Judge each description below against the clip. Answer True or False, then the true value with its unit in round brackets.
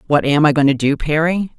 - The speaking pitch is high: False (150 Hz)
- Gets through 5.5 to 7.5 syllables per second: True (5.7 syllables/s)